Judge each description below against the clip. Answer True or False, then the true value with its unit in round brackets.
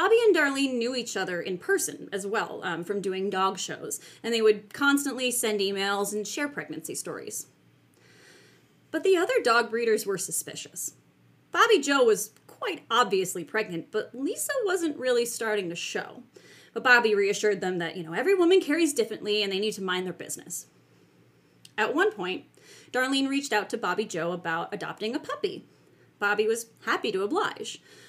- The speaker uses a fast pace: False (175 wpm)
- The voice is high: True (220 Hz)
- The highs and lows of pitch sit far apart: True (6.6 semitones)